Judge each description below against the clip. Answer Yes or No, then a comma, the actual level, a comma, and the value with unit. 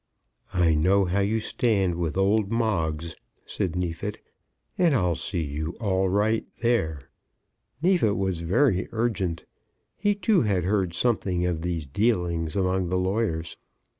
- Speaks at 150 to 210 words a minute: No, slow, 135 wpm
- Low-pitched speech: Yes, very low, 95 Hz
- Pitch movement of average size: Yes, average, 4.3 semitones